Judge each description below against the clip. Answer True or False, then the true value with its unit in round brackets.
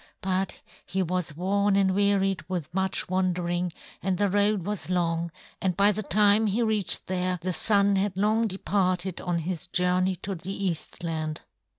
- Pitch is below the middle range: False (190 Hz)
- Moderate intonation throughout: False (2.0 semitones)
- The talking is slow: False (165 wpm)